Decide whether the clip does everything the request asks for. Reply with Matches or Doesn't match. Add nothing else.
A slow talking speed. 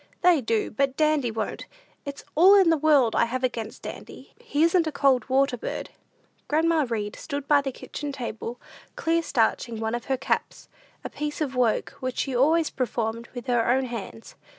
Doesn't match